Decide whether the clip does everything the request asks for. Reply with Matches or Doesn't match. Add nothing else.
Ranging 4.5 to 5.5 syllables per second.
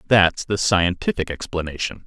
Matches